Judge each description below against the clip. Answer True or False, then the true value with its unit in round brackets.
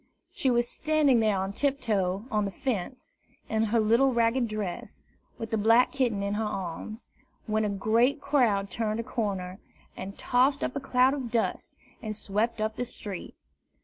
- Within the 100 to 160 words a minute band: False (175 wpm)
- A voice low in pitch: False (225 Hz)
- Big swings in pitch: False (3.5 semitones)